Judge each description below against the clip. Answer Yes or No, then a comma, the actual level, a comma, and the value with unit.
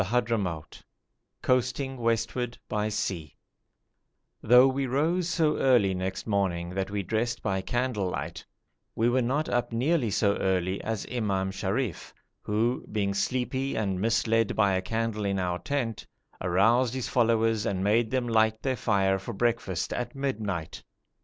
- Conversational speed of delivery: Yes, average, 150 wpm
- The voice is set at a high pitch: No, low, 110 Hz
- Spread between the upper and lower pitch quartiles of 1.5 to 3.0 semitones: No, average, 4.1 semitones